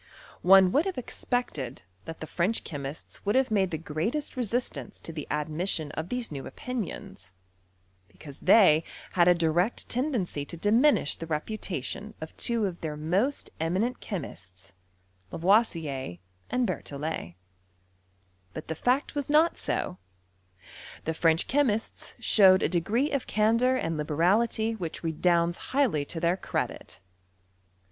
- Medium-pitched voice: Yes, medium, 180 Hz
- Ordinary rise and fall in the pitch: No, wide, 6.6 semitones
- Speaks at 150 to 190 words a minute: No, average, 140 wpm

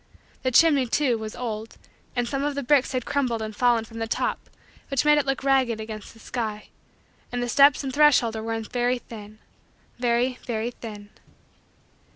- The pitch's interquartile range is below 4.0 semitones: Yes, average, 3.2 semitones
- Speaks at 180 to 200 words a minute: Yes, average, 185 wpm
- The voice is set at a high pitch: Yes, high, 240 Hz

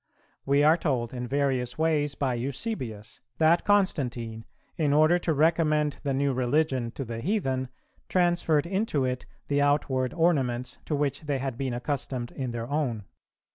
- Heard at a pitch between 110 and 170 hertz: Yes, medium, 140 Hz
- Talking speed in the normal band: Yes, average, 155 wpm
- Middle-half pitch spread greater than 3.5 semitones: Yes, average, 3.9 semitones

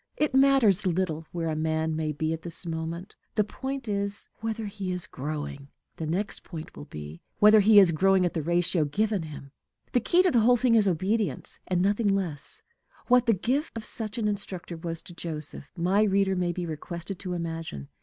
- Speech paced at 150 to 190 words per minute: No, average, 200 wpm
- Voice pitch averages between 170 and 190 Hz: Yes, medium, 185 Hz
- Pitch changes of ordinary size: Yes, average, 4.6 semitones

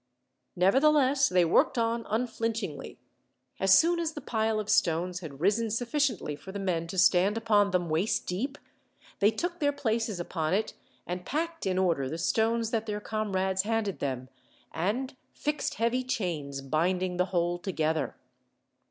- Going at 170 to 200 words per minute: No, average, 155 wpm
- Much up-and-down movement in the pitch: No, average, 4.7 semitones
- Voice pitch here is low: No, high, 200 Hz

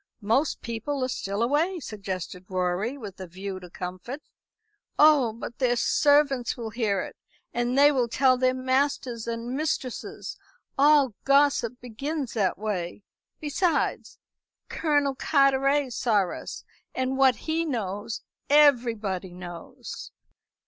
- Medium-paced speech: No, slow, 125 wpm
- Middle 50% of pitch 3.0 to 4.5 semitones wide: No, average, 5.3 semitones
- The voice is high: Yes, very high, 250 Hz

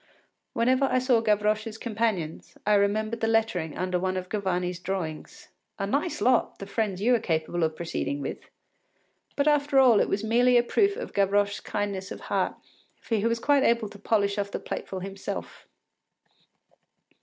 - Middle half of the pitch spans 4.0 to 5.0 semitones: No, average, 3.6 semitones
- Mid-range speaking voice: No, high, 210 Hz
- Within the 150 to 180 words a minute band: Yes, average, 170 wpm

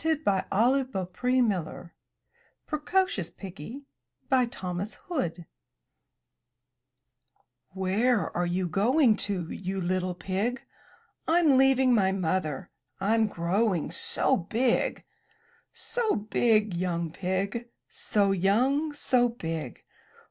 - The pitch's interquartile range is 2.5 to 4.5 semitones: No, wide, 5.5 semitones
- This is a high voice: Yes, high, 200 Hz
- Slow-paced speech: Yes, slow, 95 wpm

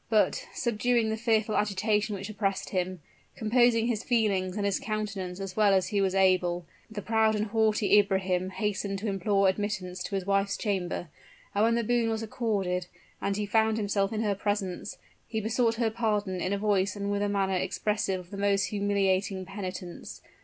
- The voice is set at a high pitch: Yes, high, 205 Hz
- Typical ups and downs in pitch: No, narrow, 2.2 semitones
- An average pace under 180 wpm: No, average, 185 wpm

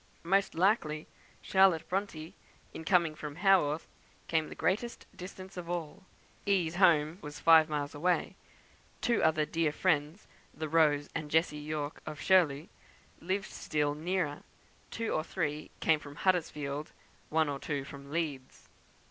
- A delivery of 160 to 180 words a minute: No, average, 140 wpm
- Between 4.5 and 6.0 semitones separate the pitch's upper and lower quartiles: No, average, 3.4 semitones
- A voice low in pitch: No, medium, 160 Hz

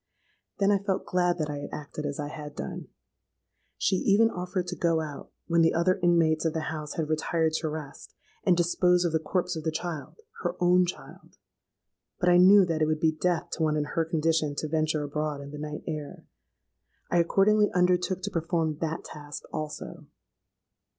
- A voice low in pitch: No, medium, 165 Hz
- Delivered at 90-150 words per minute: No, average, 190 wpm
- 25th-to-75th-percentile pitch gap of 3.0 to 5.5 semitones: No, narrow, 2.6 semitones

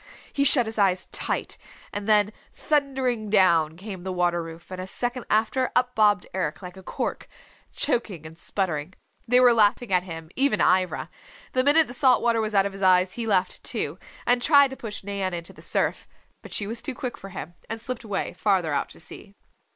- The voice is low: No, high, 205 Hz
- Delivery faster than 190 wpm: Yes, fast, 205 wpm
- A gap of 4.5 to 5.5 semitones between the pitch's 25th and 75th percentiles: Yes, average, 4.9 semitones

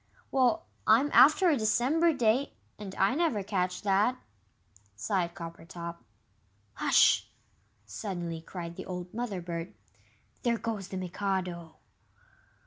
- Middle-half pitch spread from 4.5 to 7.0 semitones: Yes, wide, 5.4 semitones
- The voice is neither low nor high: No, high, 195 Hz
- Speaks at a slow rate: Yes, slow, 115 wpm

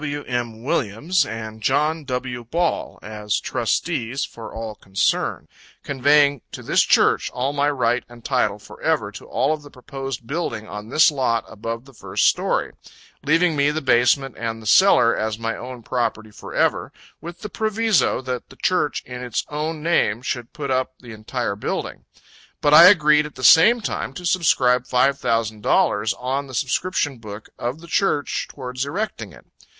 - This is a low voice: Yes, low, 130 Hz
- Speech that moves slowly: No, average, 170 wpm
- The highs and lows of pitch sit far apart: No, average, 4.5 semitones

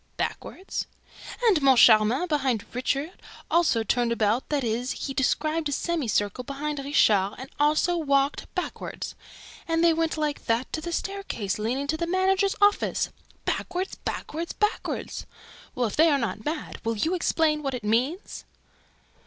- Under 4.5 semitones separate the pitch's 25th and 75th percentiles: No, average, 5.3 semitones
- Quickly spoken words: No, average, 150 wpm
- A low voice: No, very high, 290 Hz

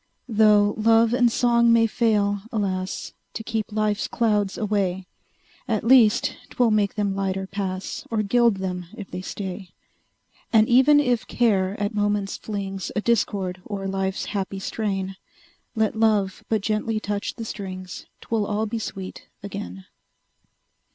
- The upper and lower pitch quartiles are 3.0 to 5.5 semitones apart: No, narrow, 2.6 semitones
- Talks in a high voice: Yes, high, 205 Hz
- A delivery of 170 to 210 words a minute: No, average, 145 wpm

